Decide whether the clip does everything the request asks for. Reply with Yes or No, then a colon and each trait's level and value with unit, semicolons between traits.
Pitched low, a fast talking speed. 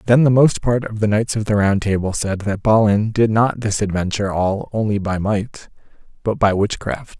Yes: low, 105 Hz; fast, 210 wpm